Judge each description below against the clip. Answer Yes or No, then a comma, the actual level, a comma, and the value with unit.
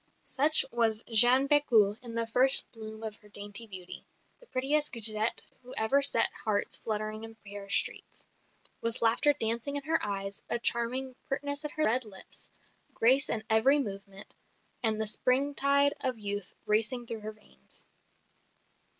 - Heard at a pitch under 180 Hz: No, high, 230 Hz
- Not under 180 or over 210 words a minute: No, average, 155 wpm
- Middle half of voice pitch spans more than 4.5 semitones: No, average, 3.8 semitones